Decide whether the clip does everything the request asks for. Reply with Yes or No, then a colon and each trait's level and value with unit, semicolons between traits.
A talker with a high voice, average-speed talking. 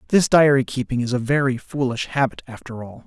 No: low, 130 Hz; average, 195 wpm